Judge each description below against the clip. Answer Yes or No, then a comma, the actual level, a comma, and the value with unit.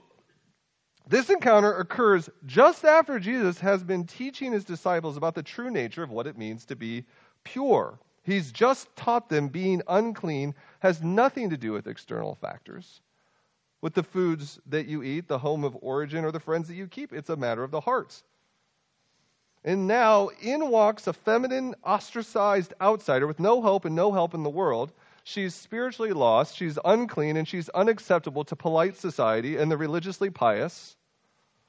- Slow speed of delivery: No, average, 170 wpm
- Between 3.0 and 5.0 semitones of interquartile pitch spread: No, wide, 5.6 semitones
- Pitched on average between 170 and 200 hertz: Yes, medium, 185 Hz